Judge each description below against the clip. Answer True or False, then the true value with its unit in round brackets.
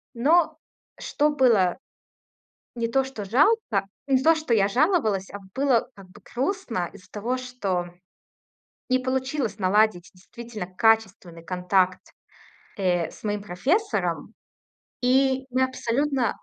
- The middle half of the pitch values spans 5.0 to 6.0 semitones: True (5.4 semitones)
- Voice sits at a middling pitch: False (235 Hz)